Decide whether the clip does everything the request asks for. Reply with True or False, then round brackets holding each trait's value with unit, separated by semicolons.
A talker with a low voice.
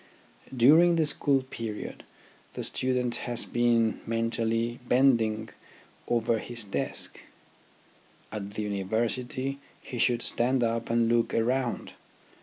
True (120 Hz)